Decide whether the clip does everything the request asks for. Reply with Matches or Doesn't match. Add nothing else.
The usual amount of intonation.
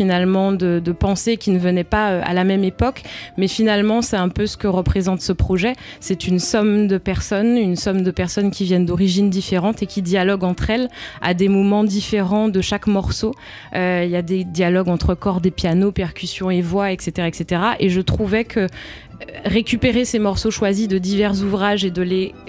Doesn't match